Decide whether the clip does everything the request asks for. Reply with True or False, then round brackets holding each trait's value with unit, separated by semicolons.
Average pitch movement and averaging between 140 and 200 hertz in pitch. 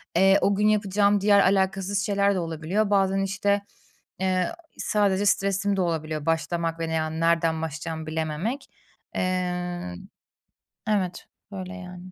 True (3.3 semitones; 185 Hz)